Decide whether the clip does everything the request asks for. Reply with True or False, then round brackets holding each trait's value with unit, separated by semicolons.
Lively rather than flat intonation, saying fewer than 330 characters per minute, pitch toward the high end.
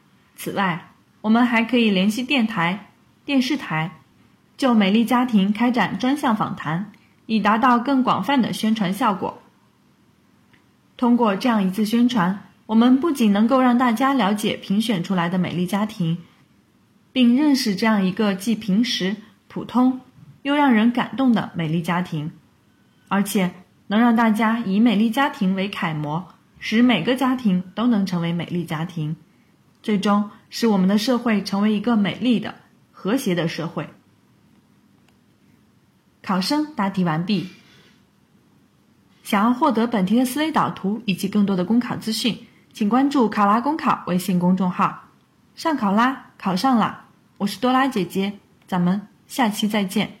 False (4.2 semitones; 225 characters per minute; 215 Hz)